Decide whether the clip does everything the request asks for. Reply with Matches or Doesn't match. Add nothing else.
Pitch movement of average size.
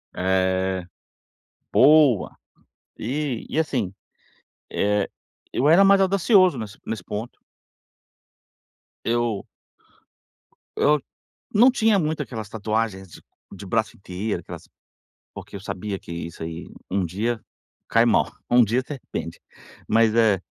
Doesn't match